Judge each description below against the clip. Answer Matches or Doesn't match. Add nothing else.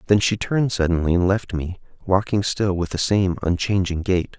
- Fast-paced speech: Doesn't match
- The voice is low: Matches